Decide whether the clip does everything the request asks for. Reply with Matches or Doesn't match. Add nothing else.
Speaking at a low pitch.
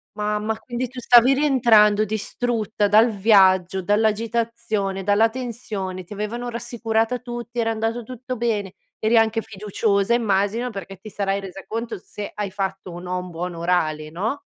Doesn't match